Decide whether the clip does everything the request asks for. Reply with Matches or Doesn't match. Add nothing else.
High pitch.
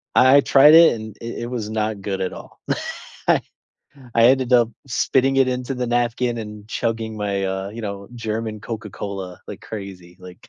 Doesn't match